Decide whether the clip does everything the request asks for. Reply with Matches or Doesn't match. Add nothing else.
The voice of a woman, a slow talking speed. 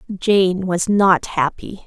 Matches